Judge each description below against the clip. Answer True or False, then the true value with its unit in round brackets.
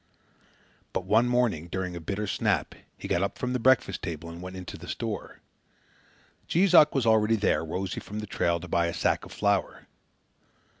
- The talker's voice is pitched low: True (100 Hz)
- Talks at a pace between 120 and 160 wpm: False (190 wpm)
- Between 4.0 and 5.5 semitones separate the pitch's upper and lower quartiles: True (4.6 semitones)